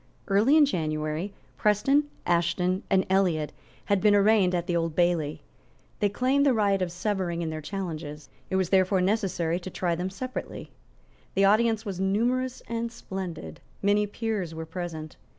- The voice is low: No, high, 190 Hz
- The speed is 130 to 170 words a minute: Yes, average, 160 wpm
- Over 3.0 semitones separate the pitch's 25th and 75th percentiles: Yes, average, 3.6 semitones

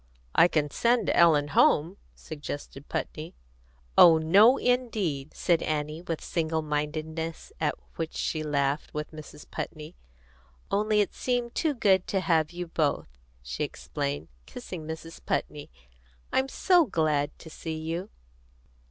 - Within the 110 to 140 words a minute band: Yes, slow, 135 wpm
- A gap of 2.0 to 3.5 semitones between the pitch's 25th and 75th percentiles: No, average, 3.9 semitones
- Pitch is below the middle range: No, medium, 160 Hz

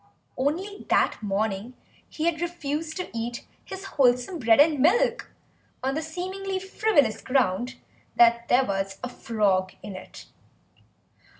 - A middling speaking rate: No, slow, 130 wpm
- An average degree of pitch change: No, wide, 7.1 semitones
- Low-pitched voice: No, very high, 265 Hz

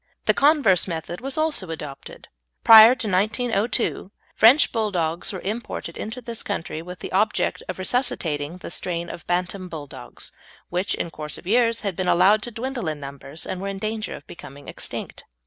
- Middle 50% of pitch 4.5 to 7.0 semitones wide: Yes, average, 5.1 semitones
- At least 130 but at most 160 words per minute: No, average, 175 wpm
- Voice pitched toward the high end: Yes, high, 195 Hz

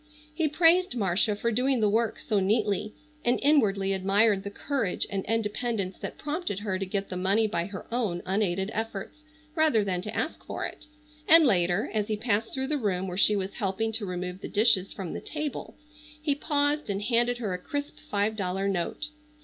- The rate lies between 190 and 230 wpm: Yes, average, 195 wpm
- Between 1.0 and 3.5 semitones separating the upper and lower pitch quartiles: No, average, 4.1 semitones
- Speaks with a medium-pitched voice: No, high, 210 Hz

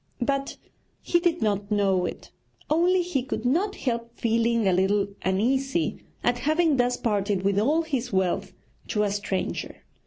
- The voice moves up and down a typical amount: No, wide, 5.7 semitones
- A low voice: No, high, 235 Hz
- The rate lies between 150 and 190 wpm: Yes, average, 155 wpm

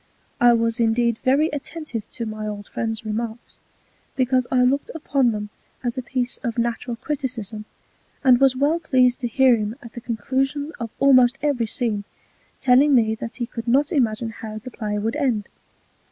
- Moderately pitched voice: No, high, 240 Hz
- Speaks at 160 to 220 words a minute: Yes, average, 175 wpm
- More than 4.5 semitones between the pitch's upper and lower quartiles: No, average, 2.8 semitones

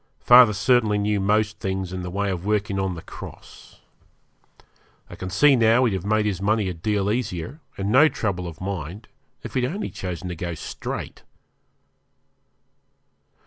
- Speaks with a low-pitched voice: Yes, low, 100 Hz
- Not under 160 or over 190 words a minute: Yes, average, 165 wpm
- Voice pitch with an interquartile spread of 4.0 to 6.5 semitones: No, average, 2.9 semitones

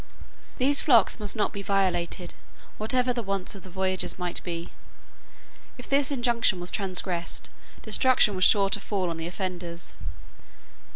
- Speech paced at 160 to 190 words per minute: No, average, 150 wpm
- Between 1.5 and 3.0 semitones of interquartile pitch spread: No, average, 4.5 semitones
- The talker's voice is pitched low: No, high, 195 Hz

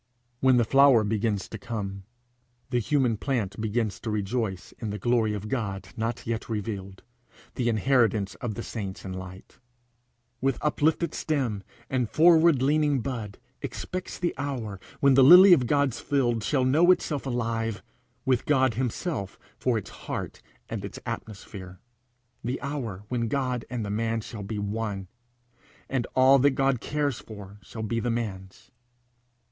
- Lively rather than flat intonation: No, average, 4.4 semitones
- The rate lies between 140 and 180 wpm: Yes, average, 155 wpm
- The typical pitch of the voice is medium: No, low, 115 Hz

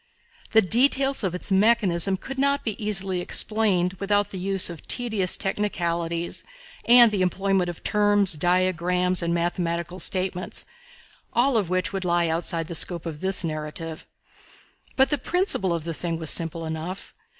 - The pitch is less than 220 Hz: Yes, medium, 185 Hz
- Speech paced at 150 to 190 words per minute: Yes, average, 155 wpm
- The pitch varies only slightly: No, average, 3.4 semitones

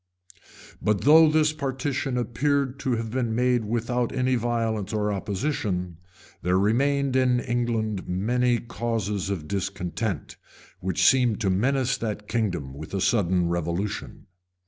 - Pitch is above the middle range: No, low, 115 Hz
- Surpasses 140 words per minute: No, slow, 135 wpm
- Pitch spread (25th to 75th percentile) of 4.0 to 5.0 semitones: Yes, average, 4.4 semitones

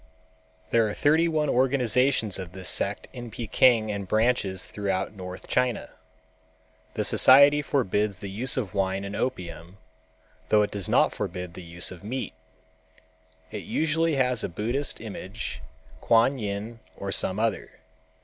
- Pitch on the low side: Yes, low, 110 Hz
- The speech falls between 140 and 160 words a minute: Yes, average, 145 wpm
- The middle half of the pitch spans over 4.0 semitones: Yes, average, 4.8 semitones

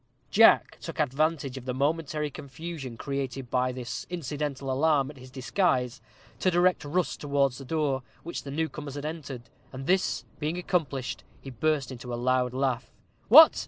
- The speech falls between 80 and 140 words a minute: No, average, 170 wpm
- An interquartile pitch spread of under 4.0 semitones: Yes, average, 3.3 semitones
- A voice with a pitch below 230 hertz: Yes, medium, 140 Hz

